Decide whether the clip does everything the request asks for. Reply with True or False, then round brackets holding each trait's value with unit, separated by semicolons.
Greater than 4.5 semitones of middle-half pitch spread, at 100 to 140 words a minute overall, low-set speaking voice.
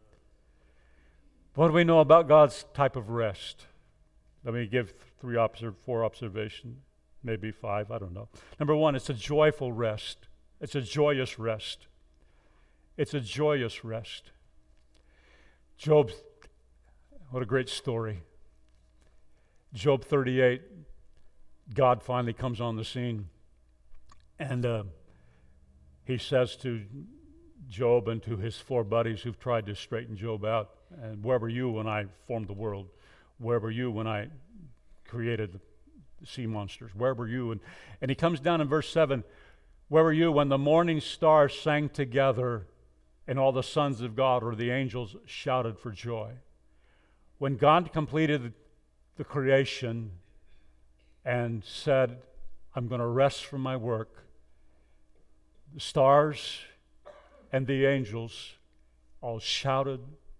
True (5.2 semitones; 135 wpm; 120 Hz)